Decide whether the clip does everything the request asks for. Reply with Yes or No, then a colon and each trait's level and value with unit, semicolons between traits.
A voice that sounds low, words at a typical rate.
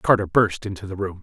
No: low, 100 Hz; fast, 245 wpm